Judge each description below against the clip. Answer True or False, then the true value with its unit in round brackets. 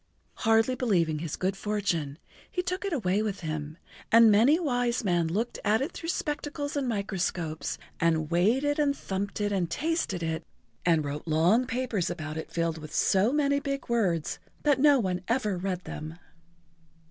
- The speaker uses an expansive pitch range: True (7.4 semitones)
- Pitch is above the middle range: True (205 Hz)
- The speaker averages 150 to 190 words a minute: True (170 wpm)